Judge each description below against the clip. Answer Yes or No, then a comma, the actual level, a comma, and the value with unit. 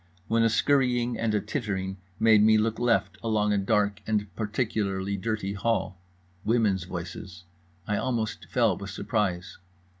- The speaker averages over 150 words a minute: No, average, 145 wpm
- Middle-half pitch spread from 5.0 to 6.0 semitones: No, narrow, 2.6 semitones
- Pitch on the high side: No, low, 105 Hz